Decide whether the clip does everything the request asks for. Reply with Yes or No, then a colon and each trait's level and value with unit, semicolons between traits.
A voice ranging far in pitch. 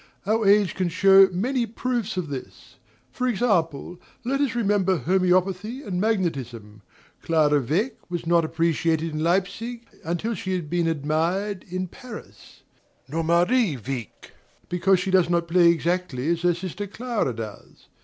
No: average, 3.9 semitones